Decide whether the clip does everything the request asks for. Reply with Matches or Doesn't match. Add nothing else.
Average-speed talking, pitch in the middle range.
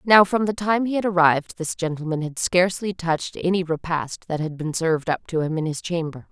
Doesn't match